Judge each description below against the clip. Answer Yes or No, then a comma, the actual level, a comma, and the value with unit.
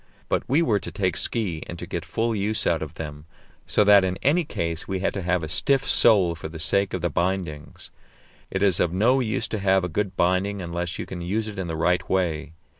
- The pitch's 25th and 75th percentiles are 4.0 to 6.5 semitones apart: No, average, 3.3 semitones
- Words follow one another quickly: Yes, fast, 240 wpm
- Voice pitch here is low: Yes, very low, 95 Hz